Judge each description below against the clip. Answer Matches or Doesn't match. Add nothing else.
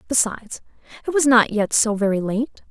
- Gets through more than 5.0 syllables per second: Matches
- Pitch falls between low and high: Doesn't match